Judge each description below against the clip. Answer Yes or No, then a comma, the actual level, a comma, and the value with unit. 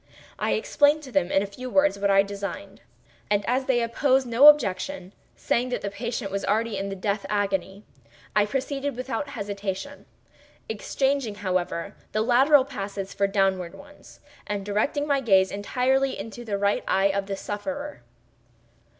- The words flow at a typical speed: Yes, average, 160 wpm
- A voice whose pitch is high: Yes, high, 210 Hz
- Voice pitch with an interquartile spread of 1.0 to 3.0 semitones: No, average, 5.1 semitones